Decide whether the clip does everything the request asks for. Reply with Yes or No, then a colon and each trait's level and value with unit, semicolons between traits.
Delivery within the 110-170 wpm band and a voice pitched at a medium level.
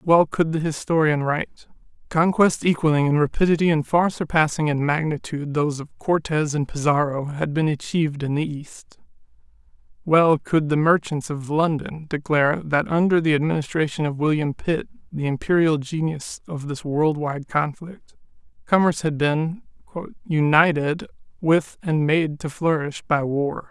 Yes: average, 145 wpm; medium, 155 Hz